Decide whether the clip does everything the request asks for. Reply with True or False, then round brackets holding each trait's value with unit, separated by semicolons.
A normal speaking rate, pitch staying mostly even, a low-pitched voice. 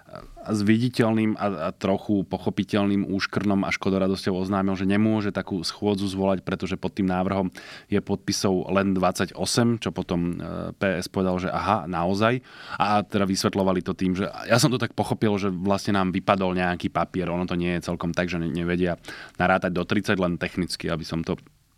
False (175 wpm; 2.0 semitones; 95 Hz)